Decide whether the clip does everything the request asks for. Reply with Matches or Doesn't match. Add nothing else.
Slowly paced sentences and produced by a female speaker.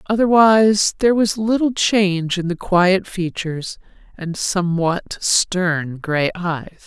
Matches